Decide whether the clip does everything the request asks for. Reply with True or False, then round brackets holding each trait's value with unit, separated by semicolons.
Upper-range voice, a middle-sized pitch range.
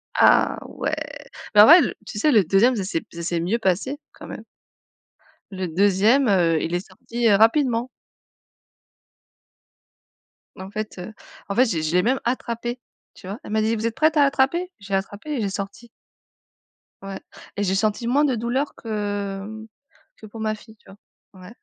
True (215 Hz; 3.7 semitones)